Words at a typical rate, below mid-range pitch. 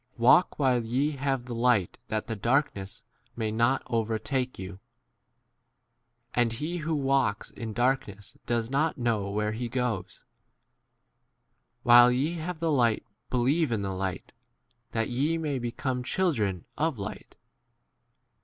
Yes: average, 150 wpm; low, 120 Hz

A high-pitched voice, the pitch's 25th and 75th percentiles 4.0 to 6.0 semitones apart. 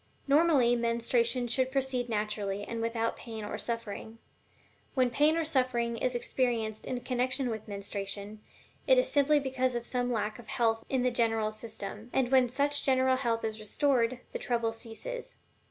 No: high, 240 Hz; narrow, 2.6 semitones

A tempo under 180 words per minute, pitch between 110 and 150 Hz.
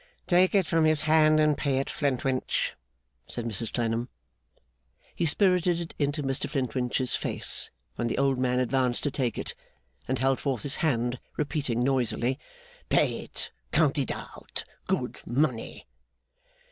Yes: average, 145 wpm; low, 135 Hz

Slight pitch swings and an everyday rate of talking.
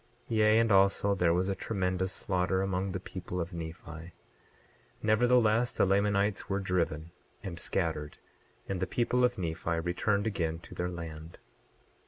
No: average, 3.2 semitones; average, 155 wpm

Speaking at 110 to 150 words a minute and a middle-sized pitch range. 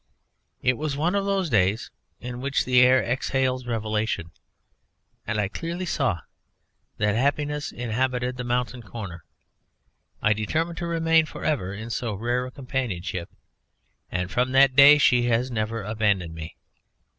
Yes: average, 145 wpm; average, 4.4 semitones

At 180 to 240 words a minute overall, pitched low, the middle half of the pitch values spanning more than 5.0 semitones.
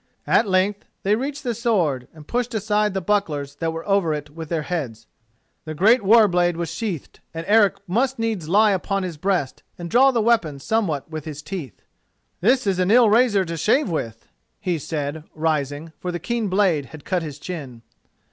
No: average, 195 wpm; medium, 180 Hz; wide, 5.4 semitones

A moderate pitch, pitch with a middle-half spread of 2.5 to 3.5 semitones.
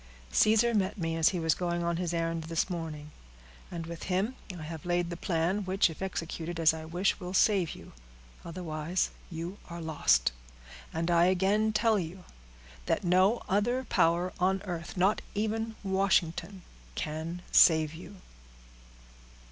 Yes: medium, 175 Hz; average, 2.8 semitones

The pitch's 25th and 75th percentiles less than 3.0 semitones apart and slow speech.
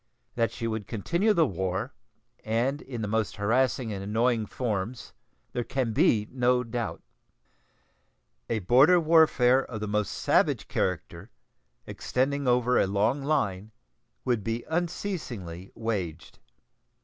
No: average, 4.0 semitones; slow, 125 wpm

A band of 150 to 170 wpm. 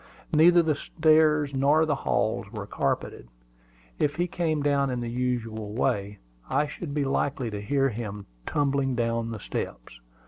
Yes: average, 160 wpm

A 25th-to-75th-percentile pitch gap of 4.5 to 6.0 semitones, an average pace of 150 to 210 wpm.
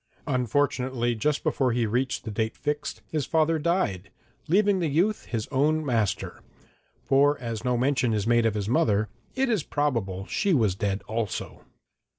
Yes: average, 5.1 semitones; average, 165 wpm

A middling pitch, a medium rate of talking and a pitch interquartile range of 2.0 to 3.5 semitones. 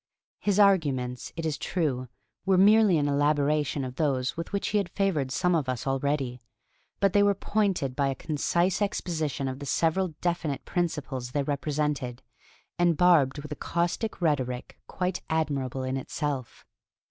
No: medium, 150 Hz; average, 160 wpm; average, 4.7 semitones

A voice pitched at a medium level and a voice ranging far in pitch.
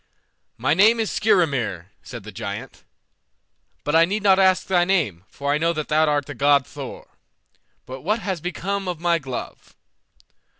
Yes: medium, 160 Hz; wide, 5.8 semitones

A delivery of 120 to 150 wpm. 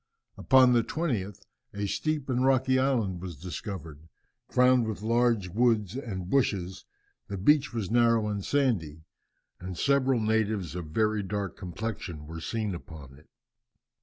Yes: average, 140 wpm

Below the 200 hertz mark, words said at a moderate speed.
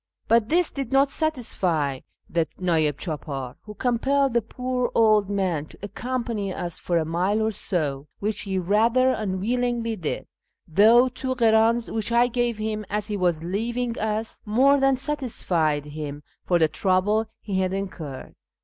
No: high, 215 Hz; average, 160 wpm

